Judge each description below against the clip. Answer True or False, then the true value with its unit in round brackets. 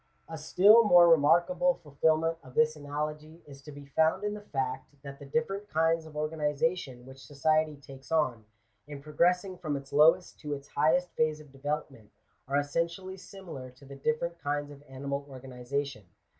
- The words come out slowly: False (170 wpm)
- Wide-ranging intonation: False (3.1 semitones)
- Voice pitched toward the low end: False (150 Hz)